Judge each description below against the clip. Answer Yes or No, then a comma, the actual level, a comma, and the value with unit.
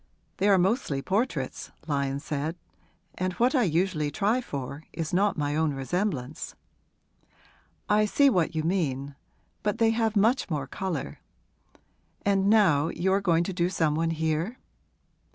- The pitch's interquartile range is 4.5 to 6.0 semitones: Yes, average, 5.3 semitones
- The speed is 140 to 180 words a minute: Yes, average, 150 wpm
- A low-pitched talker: No, medium, 175 Hz